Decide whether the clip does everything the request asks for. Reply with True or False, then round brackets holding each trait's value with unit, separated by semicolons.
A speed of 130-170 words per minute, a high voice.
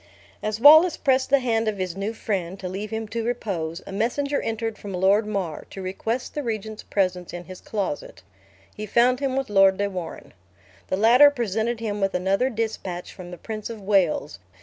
False (195 wpm; 210 Hz)